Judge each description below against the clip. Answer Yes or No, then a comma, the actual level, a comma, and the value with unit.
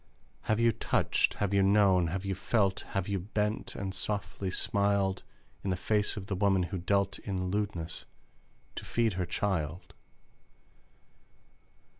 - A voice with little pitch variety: Yes, narrow, 1.8 semitones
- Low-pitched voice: Yes, low, 100 Hz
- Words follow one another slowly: No, average, 145 wpm